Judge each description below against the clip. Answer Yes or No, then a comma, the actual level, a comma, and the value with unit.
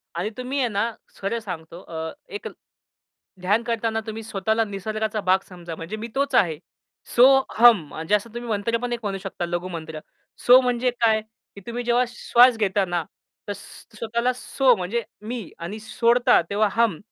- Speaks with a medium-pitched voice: No, high, 220 Hz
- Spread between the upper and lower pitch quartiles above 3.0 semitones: Yes, average, 3.8 semitones